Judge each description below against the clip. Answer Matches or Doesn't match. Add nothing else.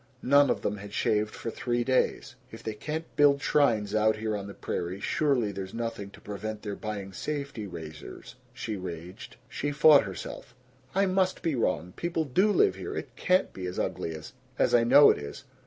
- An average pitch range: Doesn't match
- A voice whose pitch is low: Matches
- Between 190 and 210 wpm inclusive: Matches